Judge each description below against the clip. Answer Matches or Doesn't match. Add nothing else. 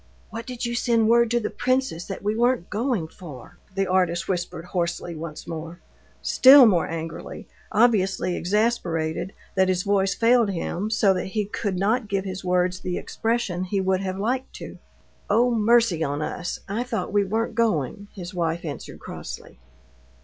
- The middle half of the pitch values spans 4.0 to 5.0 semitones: Matches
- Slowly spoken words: Doesn't match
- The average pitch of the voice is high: Matches